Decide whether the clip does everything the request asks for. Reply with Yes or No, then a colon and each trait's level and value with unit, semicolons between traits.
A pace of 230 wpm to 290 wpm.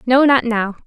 No: fast, 210 wpm